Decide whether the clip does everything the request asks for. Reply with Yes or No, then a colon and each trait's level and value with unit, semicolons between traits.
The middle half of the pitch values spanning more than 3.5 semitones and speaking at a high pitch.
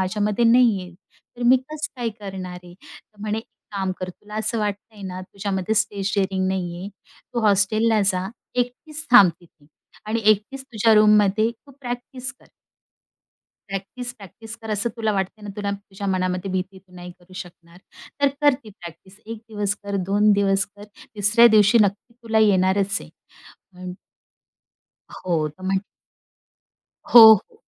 No: average, 3.0 semitones; high, 205 Hz